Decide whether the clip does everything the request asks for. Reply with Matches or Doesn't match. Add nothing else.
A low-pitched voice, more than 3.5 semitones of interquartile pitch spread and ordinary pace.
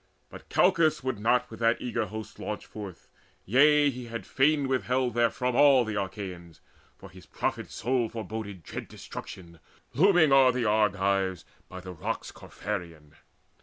Matches